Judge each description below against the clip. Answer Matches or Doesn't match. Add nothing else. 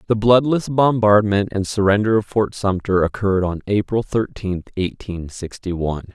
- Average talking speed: Matches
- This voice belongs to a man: Matches